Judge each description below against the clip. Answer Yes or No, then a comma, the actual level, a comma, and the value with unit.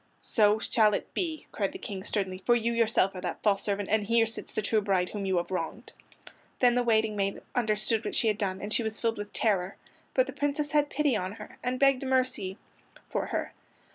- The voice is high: Yes, high, 215 Hz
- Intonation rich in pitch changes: No, average, 3.3 semitones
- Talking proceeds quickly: Yes, fast, 230 wpm